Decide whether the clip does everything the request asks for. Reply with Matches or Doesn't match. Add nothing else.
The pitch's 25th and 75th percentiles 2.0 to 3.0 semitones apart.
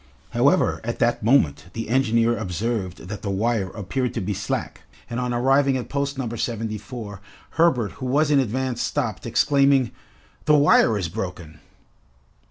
Doesn't match